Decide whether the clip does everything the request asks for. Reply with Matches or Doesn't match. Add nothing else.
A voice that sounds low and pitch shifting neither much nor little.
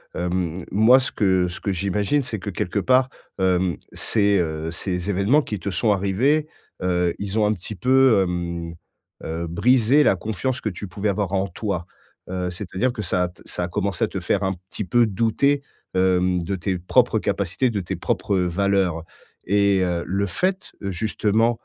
Matches